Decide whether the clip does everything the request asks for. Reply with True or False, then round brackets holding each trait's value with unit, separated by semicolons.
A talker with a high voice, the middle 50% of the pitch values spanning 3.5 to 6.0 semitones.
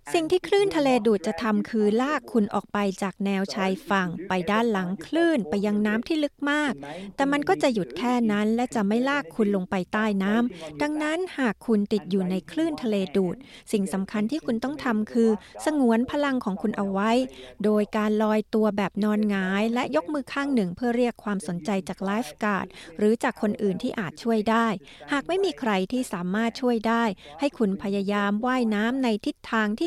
True (220 Hz; 4.0 semitones)